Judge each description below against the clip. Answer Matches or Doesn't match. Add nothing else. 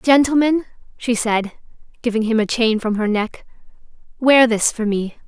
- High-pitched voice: Matches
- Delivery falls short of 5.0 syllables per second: Matches